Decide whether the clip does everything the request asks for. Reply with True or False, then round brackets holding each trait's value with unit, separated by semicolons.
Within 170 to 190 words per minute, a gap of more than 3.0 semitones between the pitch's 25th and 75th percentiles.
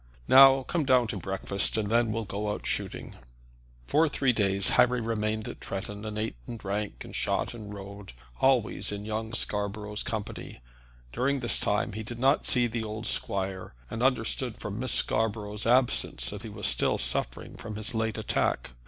False (180 wpm; 2.7 semitones)